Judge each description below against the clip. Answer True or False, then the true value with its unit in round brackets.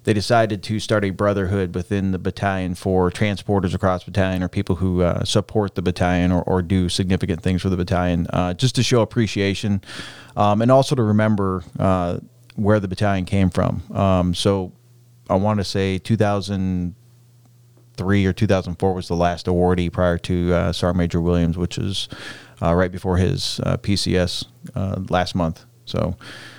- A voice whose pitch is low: True (95 Hz)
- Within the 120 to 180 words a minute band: True (170 wpm)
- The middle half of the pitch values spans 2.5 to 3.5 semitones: True (2.9 semitones)